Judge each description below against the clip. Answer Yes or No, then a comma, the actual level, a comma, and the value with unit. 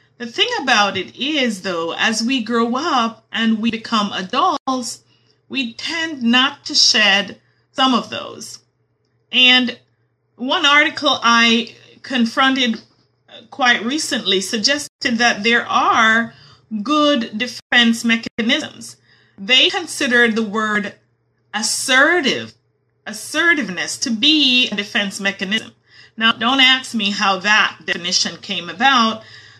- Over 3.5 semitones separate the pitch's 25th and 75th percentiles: Yes, average, 3.9 semitones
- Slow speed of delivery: Yes, slow, 115 wpm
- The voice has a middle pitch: No, high, 235 Hz